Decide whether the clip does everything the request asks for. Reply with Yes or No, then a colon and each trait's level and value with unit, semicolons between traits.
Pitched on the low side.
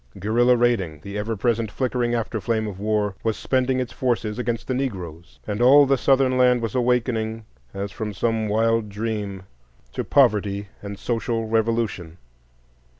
Yes: low, 115 Hz